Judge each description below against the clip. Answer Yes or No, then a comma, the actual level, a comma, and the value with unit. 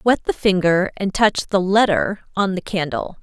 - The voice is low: No, high, 190 Hz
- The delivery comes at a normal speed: Yes, average, 185 wpm